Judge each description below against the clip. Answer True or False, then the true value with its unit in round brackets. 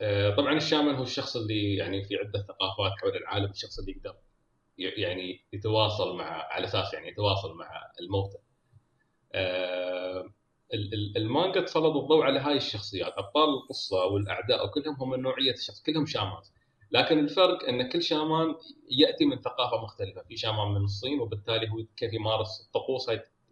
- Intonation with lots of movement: True (6.6 semitones)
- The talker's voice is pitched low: True (115 Hz)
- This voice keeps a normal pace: False (150 wpm)